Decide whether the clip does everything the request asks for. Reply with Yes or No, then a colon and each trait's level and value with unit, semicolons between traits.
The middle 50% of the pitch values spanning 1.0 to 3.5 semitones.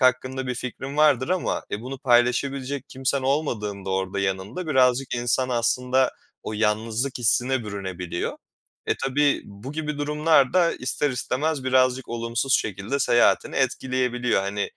Yes: average, 3.1 semitones